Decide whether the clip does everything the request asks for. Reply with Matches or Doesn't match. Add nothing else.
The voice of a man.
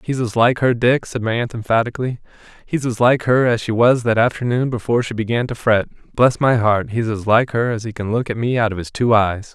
Matches